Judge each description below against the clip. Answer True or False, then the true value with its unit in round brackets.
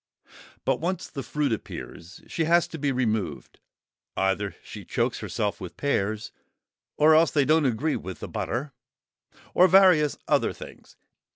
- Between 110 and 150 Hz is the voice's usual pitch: True (140 Hz)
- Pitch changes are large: True (6.7 semitones)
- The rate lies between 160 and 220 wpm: False (150 wpm)